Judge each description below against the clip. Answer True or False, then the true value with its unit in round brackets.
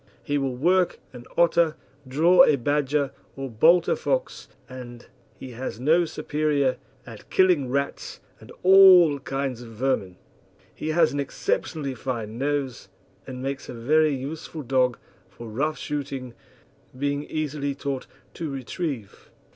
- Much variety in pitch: False (3.3 semitones)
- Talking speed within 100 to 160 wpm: True (140 wpm)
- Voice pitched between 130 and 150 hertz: True (140 Hz)